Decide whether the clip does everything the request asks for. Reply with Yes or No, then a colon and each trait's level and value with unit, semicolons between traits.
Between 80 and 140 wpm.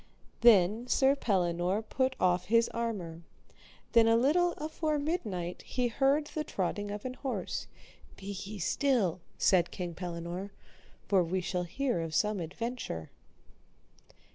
Yes: slow, 135 wpm